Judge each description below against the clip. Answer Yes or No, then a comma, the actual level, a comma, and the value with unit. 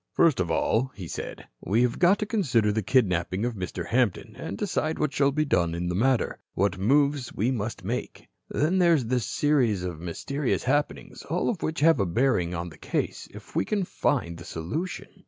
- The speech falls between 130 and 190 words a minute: No, fast, 205 wpm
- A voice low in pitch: Yes, low, 120 Hz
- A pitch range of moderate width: No, wide, 8.2 semitones